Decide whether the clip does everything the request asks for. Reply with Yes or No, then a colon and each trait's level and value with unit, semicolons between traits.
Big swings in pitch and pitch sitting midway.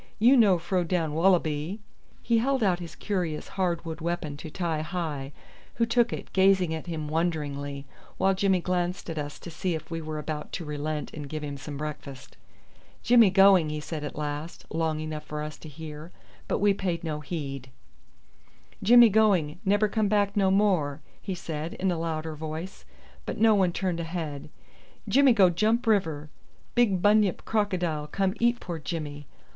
No: average, 4.2 semitones; medium, 170 Hz